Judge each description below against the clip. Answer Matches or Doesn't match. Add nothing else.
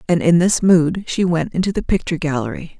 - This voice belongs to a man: Doesn't match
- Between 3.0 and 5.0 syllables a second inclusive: Doesn't match